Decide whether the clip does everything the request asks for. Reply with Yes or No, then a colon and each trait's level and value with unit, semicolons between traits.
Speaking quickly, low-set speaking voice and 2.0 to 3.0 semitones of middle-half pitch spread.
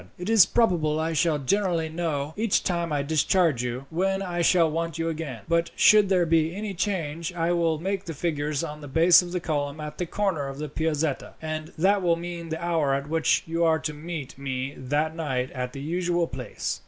No: fast, 215 wpm; medium, 165 Hz; average, 2.7 semitones